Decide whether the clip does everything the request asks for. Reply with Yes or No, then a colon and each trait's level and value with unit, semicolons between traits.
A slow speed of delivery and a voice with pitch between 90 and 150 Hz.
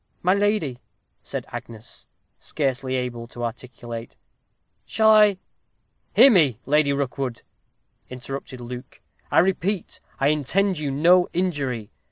Yes: slow, 120 wpm; medium, 140 Hz